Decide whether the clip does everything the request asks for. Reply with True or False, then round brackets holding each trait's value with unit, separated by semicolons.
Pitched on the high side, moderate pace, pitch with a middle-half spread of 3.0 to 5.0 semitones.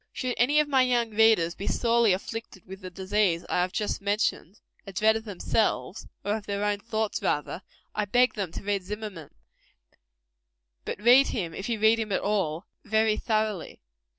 False (210 Hz; 180 wpm; 2.6 semitones)